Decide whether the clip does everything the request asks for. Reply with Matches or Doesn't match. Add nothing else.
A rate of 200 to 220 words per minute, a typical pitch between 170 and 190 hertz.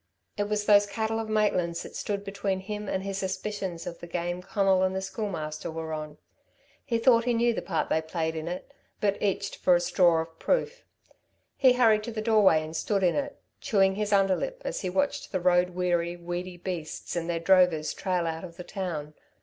Matches